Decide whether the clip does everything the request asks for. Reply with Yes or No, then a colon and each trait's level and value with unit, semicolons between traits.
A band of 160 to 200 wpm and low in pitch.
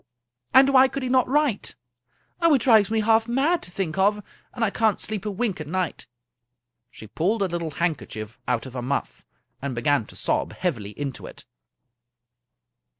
No: average, 180 wpm; high, 195 Hz